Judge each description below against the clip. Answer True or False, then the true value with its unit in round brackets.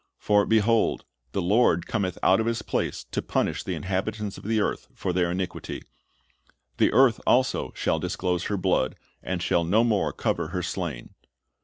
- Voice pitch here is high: False (95 Hz)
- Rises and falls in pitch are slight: False (3.5 semitones)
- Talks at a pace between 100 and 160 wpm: False (170 wpm)